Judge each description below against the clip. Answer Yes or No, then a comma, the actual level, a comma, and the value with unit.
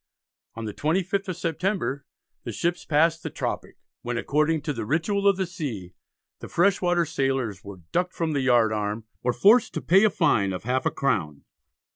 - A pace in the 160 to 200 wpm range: Yes, average, 190 wpm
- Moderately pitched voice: Yes, medium, 150 Hz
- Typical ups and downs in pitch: No, wide, 7.5 semitones